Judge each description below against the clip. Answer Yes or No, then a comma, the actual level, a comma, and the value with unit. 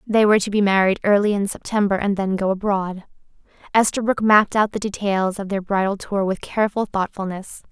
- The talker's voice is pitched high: Yes, high, 200 Hz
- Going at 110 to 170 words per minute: No, average, 185 wpm